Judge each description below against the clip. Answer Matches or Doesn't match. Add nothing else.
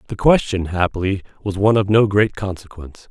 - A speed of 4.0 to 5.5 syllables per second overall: Doesn't match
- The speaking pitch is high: Doesn't match